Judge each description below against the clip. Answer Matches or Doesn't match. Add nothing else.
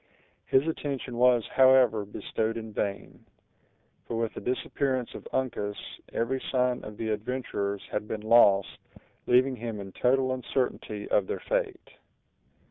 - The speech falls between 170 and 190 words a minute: Doesn't match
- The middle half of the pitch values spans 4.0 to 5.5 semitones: Doesn't match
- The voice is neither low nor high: Doesn't match